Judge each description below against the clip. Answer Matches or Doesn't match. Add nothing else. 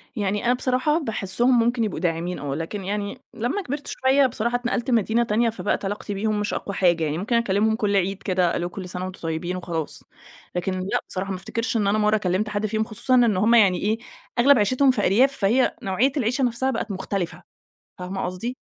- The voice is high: Matches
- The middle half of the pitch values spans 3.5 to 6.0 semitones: Matches